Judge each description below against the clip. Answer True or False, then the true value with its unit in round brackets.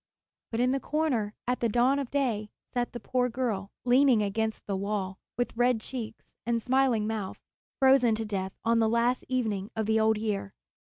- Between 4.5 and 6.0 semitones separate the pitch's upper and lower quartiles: False (2.8 semitones)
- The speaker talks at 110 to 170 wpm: False (185 wpm)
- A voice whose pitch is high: True (230 Hz)